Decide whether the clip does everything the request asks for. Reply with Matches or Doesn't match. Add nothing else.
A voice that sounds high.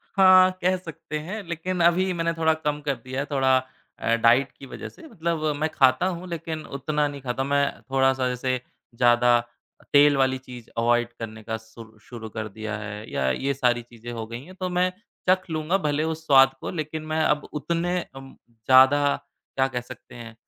Doesn't match